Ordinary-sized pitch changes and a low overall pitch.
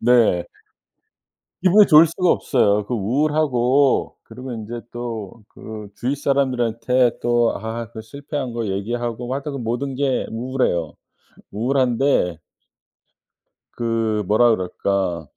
Yes: average, 3.4 semitones; low, 120 Hz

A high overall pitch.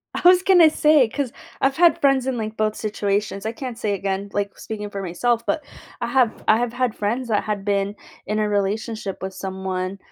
Yes: high, 215 Hz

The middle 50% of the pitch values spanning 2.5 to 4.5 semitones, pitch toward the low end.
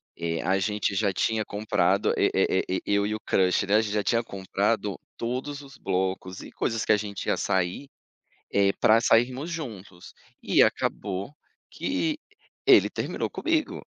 Yes: average, 3.5 semitones; low, 105 Hz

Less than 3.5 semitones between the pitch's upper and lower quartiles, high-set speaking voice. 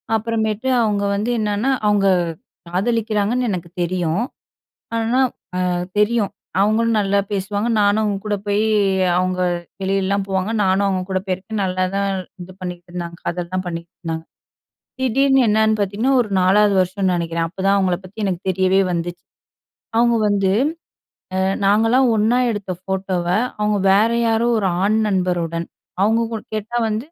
Yes: average, 2.8 semitones; high, 200 Hz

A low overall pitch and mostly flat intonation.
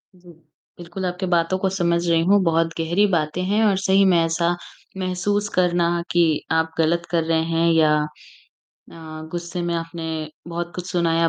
No: medium, 170 Hz; narrow, 1.7 semitones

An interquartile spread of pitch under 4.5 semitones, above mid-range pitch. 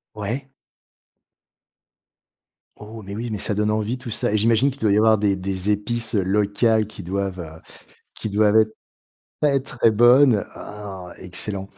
No: narrow, 2.4 semitones; low, 105 Hz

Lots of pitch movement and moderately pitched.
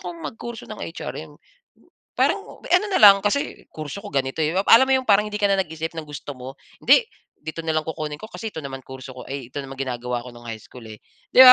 Yes: wide, 7.4 semitones; medium, 155 Hz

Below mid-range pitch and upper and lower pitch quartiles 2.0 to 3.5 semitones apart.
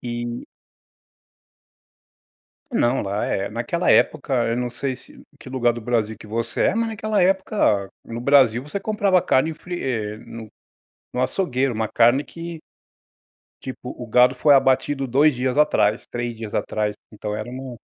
No: low, 125 Hz; average, 4.2 semitones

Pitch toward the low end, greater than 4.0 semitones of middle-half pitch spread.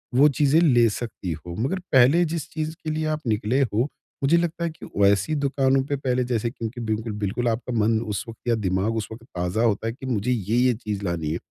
Yes: low, 120 Hz; average, 4.5 semitones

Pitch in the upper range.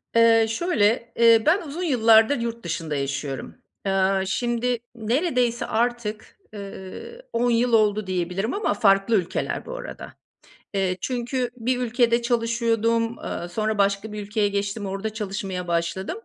Yes: high, 225 Hz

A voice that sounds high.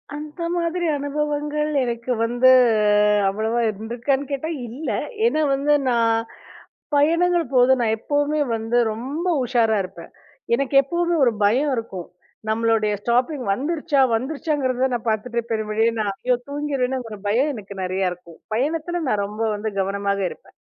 Yes: very high, 250 Hz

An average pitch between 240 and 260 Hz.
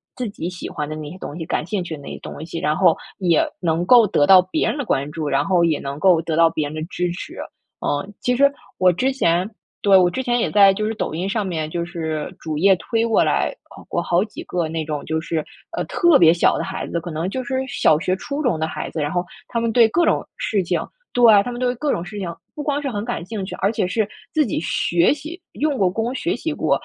No: medium, 185 Hz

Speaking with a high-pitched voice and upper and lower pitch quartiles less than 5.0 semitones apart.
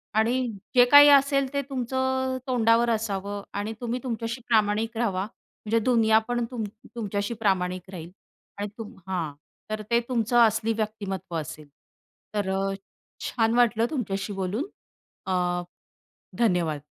Yes: high, 225 Hz; average, 3.6 semitones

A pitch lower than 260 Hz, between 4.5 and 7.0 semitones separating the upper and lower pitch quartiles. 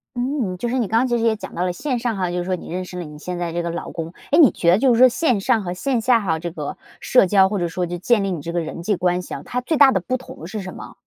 Yes: high, 190 Hz; wide, 5.5 semitones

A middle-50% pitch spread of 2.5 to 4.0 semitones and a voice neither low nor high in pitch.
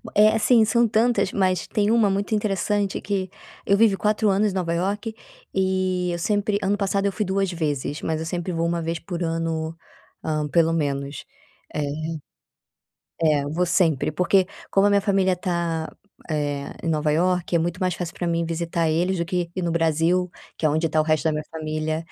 Yes: average, 3.3 semitones; medium, 175 Hz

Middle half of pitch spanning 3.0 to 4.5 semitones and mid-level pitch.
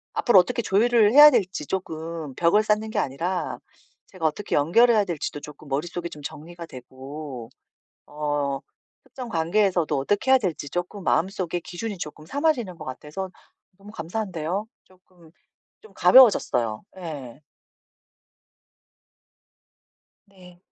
No: wide, 5.5 semitones; medium, 175 Hz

